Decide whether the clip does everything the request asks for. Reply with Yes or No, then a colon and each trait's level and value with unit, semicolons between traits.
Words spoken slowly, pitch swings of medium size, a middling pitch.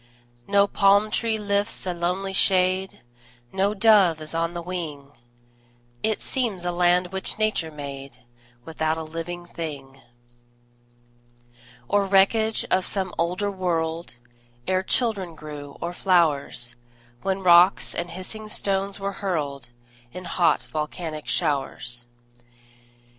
Yes: slow, 120 wpm; average, 3.7 semitones; medium, 180 Hz